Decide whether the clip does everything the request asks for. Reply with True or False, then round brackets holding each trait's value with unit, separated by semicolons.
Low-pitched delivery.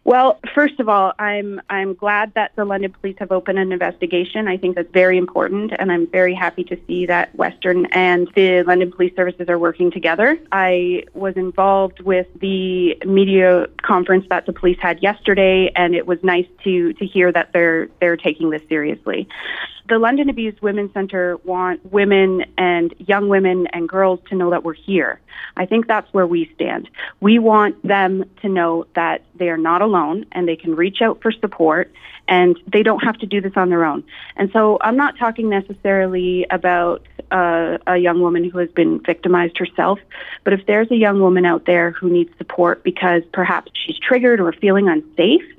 False (185 Hz)